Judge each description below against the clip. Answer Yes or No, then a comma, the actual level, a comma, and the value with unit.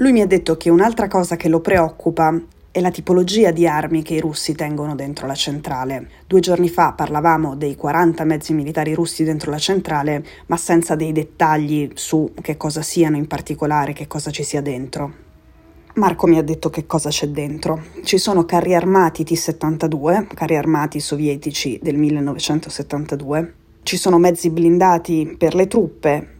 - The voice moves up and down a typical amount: No, narrow, 2.2 semitones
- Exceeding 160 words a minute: Yes, fast, 170 wpm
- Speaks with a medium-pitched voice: Yes, medium, 160 Hz